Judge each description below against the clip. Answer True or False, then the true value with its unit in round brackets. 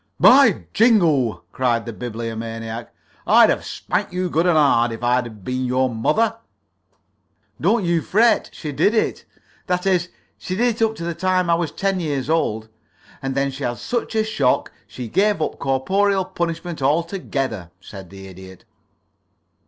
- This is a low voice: False (150 Hz)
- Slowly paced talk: False (160 wpm)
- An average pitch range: False (7.6 semitones)